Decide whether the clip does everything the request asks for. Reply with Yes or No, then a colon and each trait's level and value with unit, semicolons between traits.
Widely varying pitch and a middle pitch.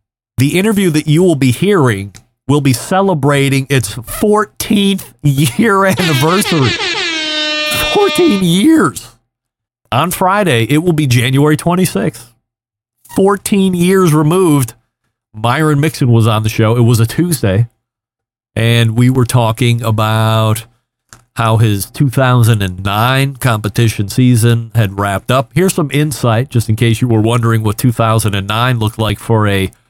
No: wide, 5.9 semitones; low, 125 Hz